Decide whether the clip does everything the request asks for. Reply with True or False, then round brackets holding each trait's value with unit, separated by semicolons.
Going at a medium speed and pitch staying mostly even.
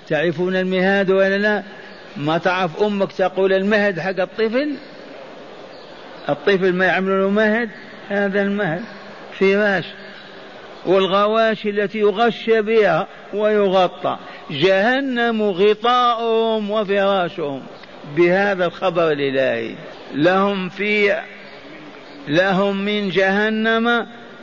True (85 wpm; 2.2 semitones)